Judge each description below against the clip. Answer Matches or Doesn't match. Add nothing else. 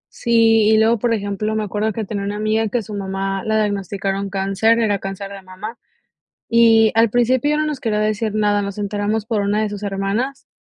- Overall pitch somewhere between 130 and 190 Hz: Doesn't match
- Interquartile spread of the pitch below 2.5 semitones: Matches